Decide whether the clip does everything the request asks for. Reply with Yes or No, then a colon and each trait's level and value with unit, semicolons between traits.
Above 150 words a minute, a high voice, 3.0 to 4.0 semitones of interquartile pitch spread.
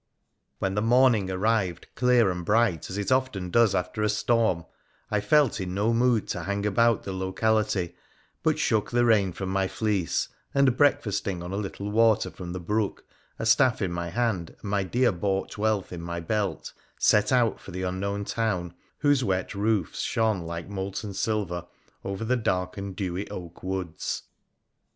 No: average, 175 wpm; low, 100 Hz; average, 3.3 semitones